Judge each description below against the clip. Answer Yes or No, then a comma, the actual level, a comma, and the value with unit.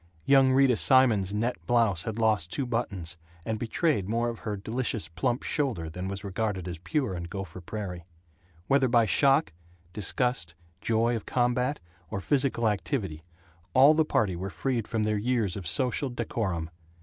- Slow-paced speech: No, average, 160 wpm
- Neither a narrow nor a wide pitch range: Yes, average, 4.9 semitones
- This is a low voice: Yes, low, 110 Hz